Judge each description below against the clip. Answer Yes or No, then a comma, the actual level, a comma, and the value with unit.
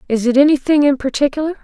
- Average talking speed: Yes, average, 185 wpm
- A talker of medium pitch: No, very high, 275 Hz